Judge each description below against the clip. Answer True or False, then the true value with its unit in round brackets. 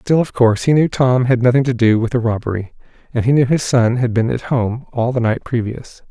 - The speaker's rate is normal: False (255 wpm)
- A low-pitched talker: True (120 Hz)